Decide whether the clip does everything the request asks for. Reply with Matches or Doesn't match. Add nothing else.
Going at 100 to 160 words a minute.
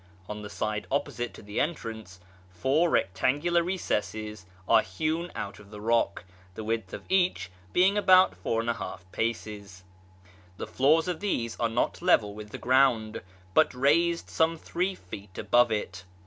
Matches